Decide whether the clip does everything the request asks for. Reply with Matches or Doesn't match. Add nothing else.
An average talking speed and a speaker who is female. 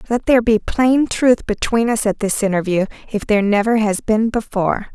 Matches